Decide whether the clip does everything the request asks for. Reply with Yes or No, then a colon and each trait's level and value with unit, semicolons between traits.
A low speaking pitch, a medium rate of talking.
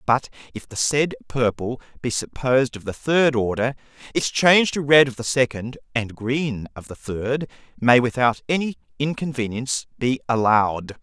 Yes: low, 125 Hz; average, 160 wpm